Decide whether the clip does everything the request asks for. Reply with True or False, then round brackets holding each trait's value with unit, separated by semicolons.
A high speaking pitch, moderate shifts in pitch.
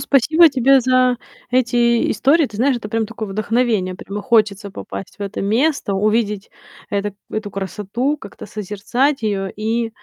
True (225 Hz; 3.8 semitones)